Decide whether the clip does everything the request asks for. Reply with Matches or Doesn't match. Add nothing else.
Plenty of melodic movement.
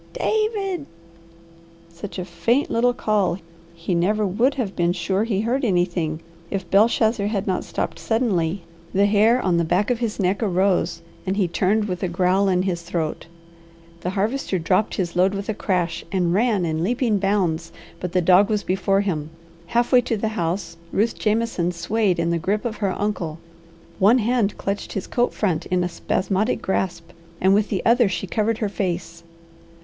Doesn't match